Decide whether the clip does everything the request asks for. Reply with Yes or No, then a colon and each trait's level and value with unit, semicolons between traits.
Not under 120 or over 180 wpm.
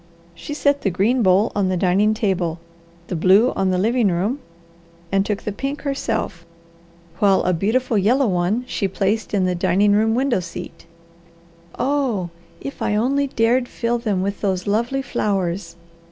Yes: average, 165 wpm